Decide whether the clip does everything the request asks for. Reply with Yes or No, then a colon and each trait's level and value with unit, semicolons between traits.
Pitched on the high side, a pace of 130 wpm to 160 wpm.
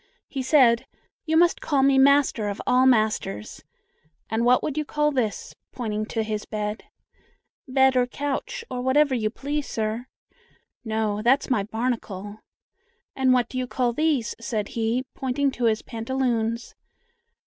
Yes: high, 245 Hz; average, 150 wpm